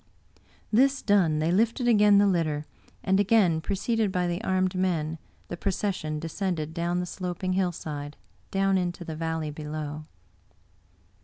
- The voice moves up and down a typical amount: Yes, average, 3.7 semitones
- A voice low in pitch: No, medium, 180 Hz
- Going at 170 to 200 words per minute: No, average, 140 wpm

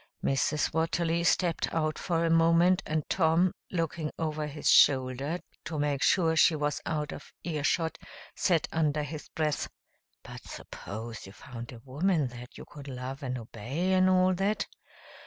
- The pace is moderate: Yes, average, 160 wpm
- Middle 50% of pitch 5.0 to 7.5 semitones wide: No, average, 3.4 semitones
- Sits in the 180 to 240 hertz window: No, medium, 155 Hz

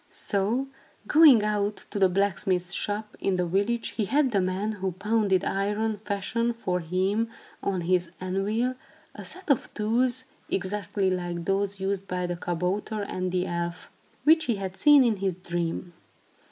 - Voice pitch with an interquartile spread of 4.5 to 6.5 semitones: No, average, 3.1 semitones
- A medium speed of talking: Yes, average, 160 wpm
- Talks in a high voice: Yes, high, 195 Hz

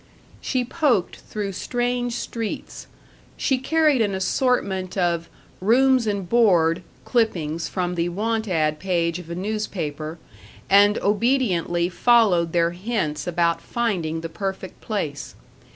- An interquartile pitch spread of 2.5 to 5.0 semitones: No, wide, 5.4 semitones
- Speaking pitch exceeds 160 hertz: Yes, high, 190 Hz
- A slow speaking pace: Yes, slow, 120 wpm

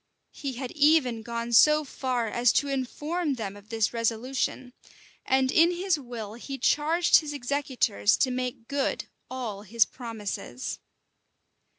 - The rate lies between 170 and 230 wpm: No, slow, 135 wpm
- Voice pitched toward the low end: No, very high, 255 Hz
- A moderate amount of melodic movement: Yes, average, 3.8 semitones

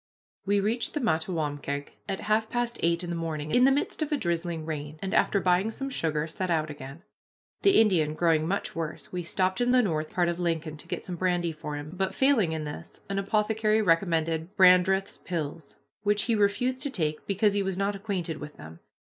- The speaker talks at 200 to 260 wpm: Yes, fast, 205 wpm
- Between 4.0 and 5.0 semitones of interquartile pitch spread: Yes, average, 4.6 semitones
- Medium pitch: Yes, medium, 180 Hz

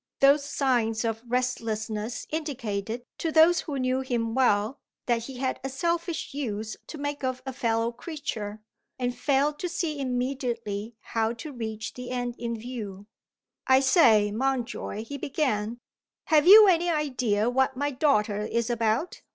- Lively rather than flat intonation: No, average, 4.0 semitones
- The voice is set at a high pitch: Yes, very high, 250 Hz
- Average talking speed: Yes, average, 155 wpm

